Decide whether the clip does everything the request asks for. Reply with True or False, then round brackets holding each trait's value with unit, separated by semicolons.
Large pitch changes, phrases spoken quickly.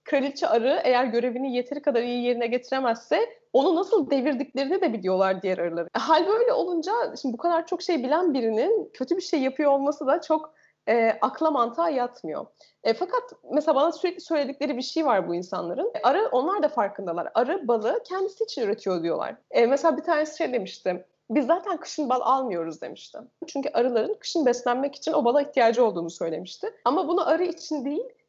True (5.8 semitones; 180 wpm)